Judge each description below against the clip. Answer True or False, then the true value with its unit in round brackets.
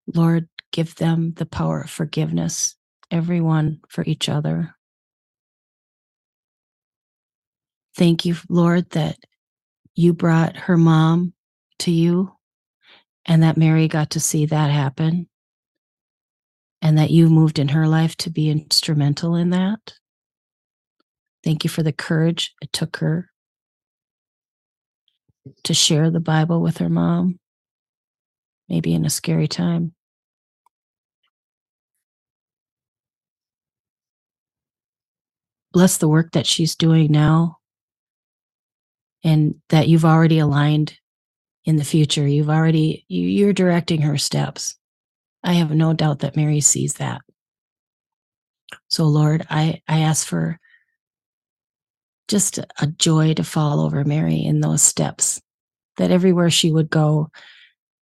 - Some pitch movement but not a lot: False (1.9 semitones)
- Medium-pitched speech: True (160 Hz)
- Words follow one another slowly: True (115 wpm)